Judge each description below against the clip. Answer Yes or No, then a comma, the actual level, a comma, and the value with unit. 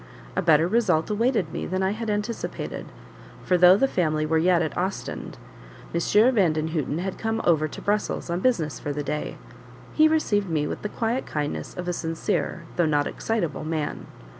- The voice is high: No, medium, 175 Hz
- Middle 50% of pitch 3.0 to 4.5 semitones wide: No, average, 5.2 semitones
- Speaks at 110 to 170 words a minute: No, average, 180 wpm